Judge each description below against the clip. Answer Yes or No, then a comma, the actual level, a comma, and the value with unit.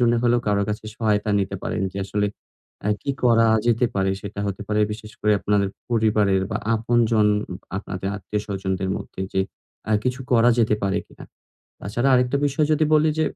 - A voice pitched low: Yes, low, 105 Hz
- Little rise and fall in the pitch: No, average, 3.0 semitones